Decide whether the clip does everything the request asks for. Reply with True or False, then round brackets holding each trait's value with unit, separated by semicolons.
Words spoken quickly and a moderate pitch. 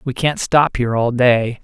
False (220 wpm; 125 Hz)